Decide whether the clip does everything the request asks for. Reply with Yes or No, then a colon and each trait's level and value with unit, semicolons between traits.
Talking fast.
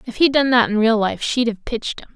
Yes: fast, 305 wpm